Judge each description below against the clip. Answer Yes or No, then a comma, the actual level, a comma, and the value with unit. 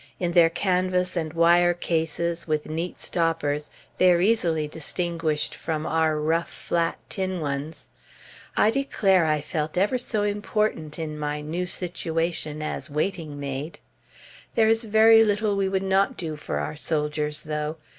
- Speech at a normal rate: Yes, average, 150 wpm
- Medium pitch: Yes, medium, 165 Hz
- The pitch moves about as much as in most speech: Yes, average, 3.5 semitones